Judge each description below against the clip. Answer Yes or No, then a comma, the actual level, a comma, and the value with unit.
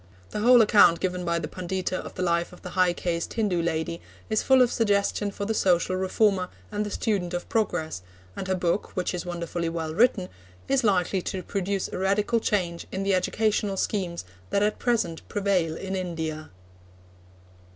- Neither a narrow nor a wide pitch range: Yes, average, 3.1 semitones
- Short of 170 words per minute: No, average, 180 wpm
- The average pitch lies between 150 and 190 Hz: Yes, medium, 185 Hz